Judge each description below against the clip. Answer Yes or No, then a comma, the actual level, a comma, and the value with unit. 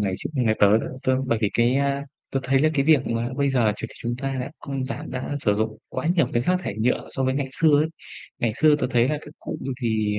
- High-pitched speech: No, low, 130 Hz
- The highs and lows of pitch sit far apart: No, average, 3.4 semitones